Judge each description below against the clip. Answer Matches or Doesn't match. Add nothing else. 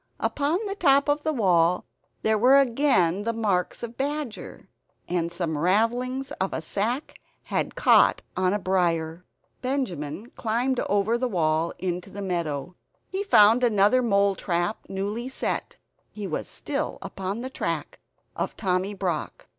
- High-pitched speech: Matches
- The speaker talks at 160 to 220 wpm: Doesn't match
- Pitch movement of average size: Doesn't match